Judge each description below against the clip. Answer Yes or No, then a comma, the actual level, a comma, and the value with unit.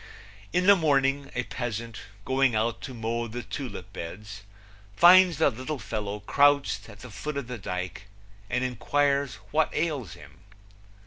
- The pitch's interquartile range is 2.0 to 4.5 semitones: No, average, 5.1 semitones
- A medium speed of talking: Yes, average, 150 wpm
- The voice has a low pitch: Yes, low, 125 Hz